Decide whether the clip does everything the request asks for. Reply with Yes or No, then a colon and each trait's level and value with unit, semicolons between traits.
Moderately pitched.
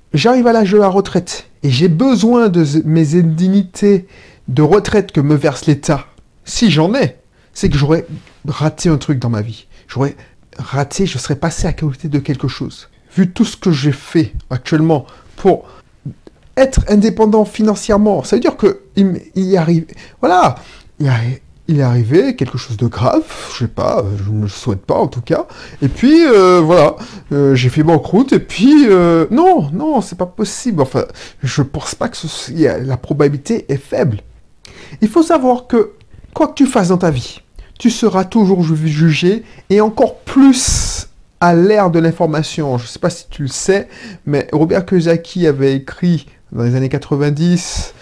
Yes: medium, 165 Hz